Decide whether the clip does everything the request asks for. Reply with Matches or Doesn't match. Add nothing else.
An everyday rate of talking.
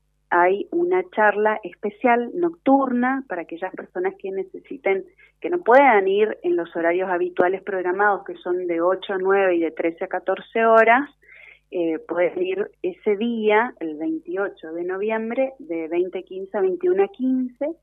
Matches